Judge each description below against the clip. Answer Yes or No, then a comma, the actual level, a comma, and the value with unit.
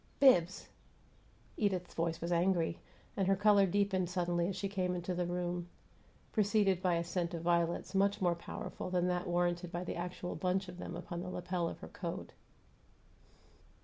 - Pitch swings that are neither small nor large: No, narrow, 1.7 semitones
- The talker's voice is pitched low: No, medium, 180 Hz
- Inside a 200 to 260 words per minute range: No, average, 175 wpm